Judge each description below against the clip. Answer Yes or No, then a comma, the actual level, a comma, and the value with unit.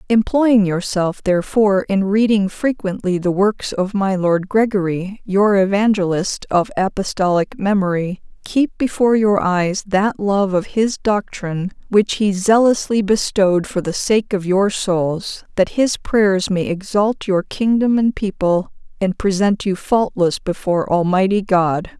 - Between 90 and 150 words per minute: Yes, average, 140 wpm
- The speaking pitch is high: Yes, high, 195 Hz